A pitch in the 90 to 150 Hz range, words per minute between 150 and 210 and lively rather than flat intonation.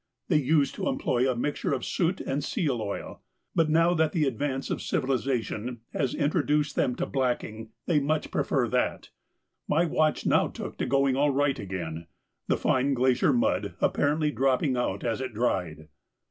No: low, 135 Hz; average, 170 wpm; average, 3.8 semitones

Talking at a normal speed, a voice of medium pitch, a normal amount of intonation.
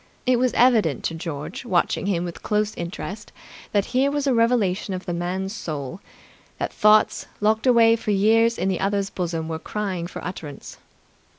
No: average, 175 wpm; high, 200 Hz; average, 4.5 semitones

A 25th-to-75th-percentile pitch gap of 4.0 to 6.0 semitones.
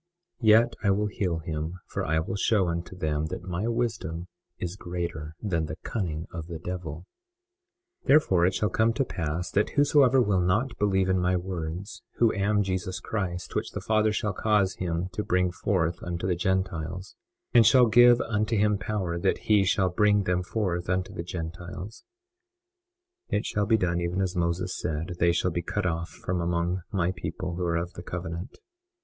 No: average, 3.2 semitones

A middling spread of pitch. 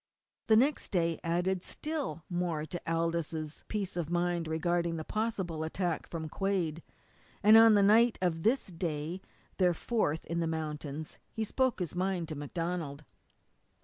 Yes: average, 3.3 semitones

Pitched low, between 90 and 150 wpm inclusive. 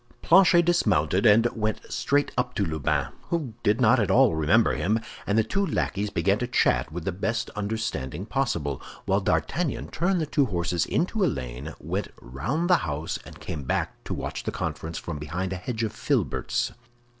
No: low, 105 Hz; average, 185 wpm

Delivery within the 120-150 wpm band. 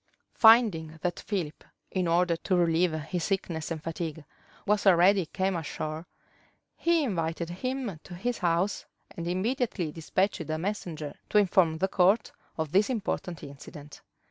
Yes: average, 145 wpm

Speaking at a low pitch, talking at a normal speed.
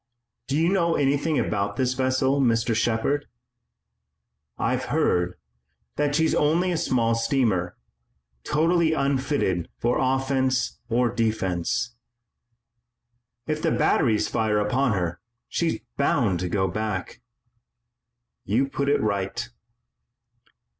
No: low, 125 Hz; slow, 110 wpm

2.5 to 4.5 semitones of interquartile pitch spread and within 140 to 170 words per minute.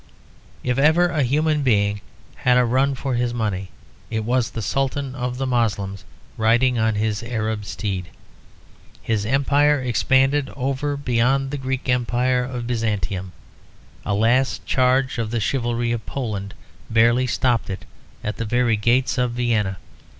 Yes: average, 3.0 semitones; average, 155 wpm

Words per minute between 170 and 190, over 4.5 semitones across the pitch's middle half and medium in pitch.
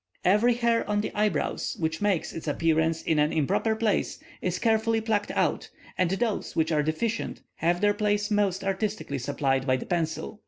No: average, 180 wpm; average, 5.0 semitones; high, 195 Hz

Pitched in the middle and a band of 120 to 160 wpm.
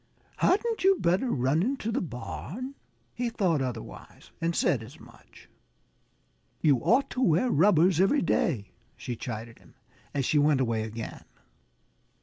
Yes: medium, 155 Hz; average, 140 wpm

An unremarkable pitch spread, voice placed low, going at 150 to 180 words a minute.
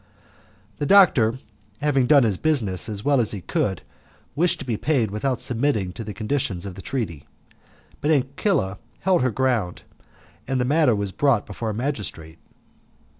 No: wide, 5.8 semitones; low, 120 Hz; average, 165 wpm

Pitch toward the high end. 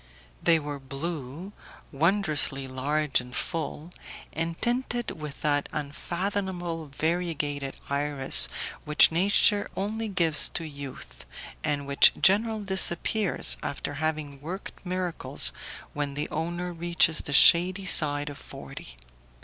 No: medium, 160 Hz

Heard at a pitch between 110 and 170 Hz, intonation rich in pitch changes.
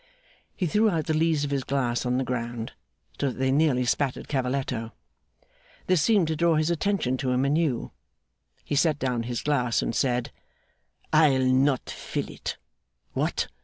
No: low, 135 Hz; average, 3.7 semitones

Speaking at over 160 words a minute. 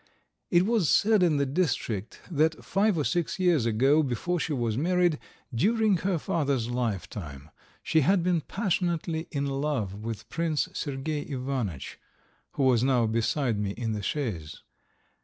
No: average, 150 wpm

